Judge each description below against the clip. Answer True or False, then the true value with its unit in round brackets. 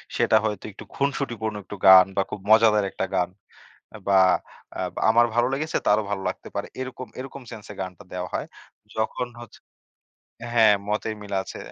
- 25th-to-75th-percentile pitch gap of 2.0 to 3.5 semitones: True (2.8 semitones)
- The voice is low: True (110 Hz)